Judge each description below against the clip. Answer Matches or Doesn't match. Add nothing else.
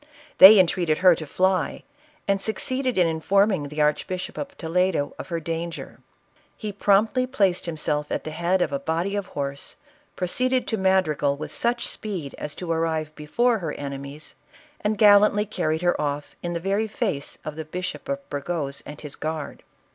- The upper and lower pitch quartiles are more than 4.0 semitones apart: Matches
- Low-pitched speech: Doesn't match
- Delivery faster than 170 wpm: Matches